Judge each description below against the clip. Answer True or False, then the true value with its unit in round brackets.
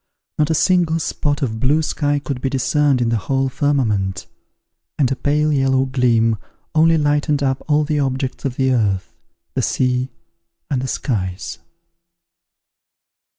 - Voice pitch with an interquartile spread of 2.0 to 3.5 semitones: True (2.9 semitones)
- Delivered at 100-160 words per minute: True (150 wpm)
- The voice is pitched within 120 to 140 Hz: True (135 Hz)